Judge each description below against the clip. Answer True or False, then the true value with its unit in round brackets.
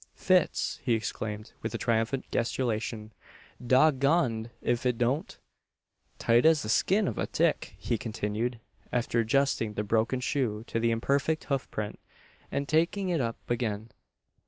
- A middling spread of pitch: True (3.7 semitones)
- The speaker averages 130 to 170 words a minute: True (150 wpm)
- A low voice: True (120 Hz)